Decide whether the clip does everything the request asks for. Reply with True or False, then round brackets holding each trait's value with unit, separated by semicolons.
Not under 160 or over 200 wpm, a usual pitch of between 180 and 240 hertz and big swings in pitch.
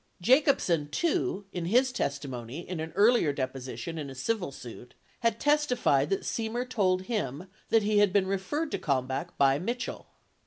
True (165 wpm; 185 Hz; 8.7 semitones)